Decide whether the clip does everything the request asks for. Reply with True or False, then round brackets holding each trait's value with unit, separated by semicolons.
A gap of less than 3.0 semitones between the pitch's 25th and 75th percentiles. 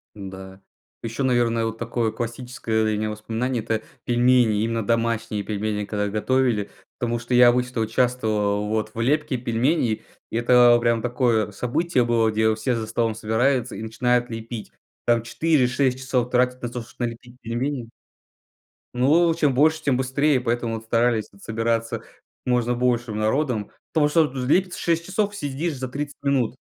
True (2.4 semitones)